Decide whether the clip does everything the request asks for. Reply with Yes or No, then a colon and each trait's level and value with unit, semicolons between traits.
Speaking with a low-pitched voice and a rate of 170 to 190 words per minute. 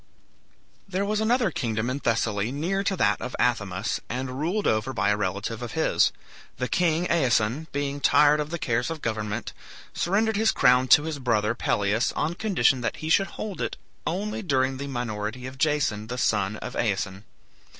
Yes: low, 130 Hz; average, 180 wpm